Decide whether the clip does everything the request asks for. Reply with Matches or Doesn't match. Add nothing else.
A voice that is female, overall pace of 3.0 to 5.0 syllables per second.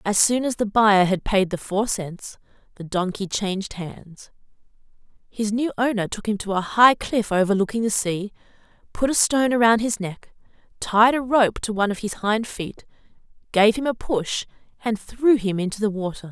Matches